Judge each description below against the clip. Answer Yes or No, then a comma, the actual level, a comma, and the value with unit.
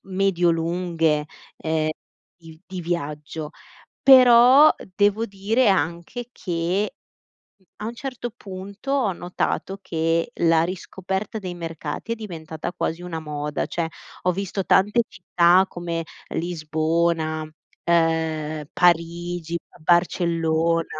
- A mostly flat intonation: No, average, 3.1 semitones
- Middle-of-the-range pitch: Yes, medium, 170 Hz